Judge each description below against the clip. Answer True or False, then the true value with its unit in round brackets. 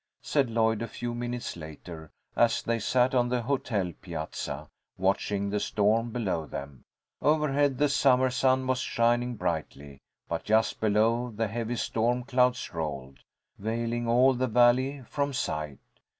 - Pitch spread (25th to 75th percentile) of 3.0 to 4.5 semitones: True (4.2 semitones)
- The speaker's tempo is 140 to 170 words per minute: True (145 wpm)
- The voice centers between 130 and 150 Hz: False (115 Hz)